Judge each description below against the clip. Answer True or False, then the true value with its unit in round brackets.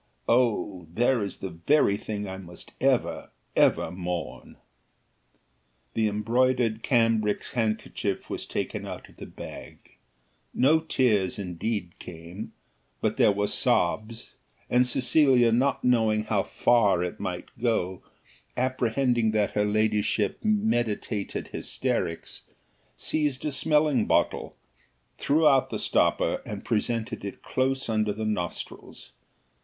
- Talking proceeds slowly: True (120 wpm)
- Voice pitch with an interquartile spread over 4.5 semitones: False (3.8 semitones)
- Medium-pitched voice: False (110 Hz)